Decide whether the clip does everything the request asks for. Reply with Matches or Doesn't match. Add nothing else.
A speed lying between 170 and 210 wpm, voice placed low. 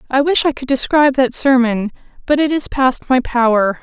Doesn't match